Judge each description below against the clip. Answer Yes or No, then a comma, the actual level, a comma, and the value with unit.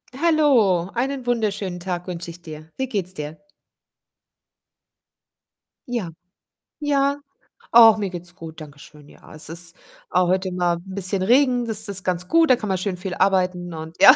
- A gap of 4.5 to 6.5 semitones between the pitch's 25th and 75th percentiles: Yes, average, 5.2 semitones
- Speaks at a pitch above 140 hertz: Yes, medium, 185 Hz